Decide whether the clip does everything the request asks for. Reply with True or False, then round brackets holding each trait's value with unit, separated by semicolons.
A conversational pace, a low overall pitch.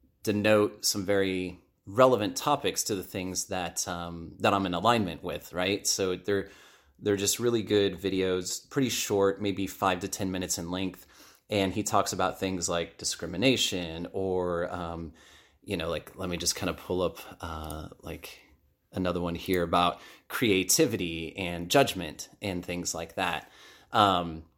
True (160 wpm; 95 Hz)